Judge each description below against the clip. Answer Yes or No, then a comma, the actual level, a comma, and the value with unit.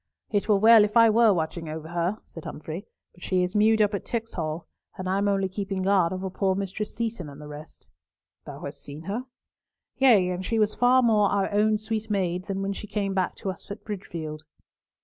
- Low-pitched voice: No, high, 195 Hz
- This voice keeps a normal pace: No, fast, 215 wpm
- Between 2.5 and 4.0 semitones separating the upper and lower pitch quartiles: Yes, average, 2.9 semitones